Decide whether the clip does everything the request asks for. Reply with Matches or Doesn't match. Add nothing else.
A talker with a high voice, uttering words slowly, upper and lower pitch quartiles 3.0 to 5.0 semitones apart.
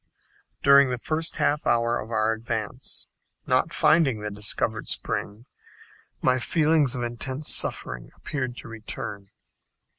Doesn't match